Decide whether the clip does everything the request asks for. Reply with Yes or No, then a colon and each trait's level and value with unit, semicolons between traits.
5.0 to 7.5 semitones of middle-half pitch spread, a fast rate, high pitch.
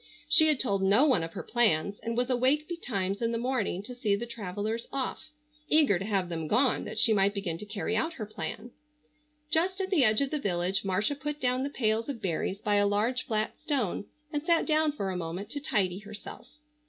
Yes: wide, 5.4 semitones; fast, 220 wpm; high, 220 Hz